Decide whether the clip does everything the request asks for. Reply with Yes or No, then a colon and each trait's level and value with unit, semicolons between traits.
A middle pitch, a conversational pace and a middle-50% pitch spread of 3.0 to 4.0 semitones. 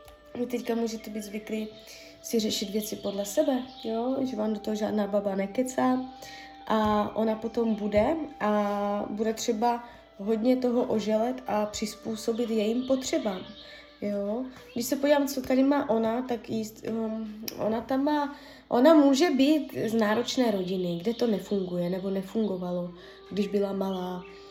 No: high, 225 Hz; average, 145 wpm; average, 3.6 semitones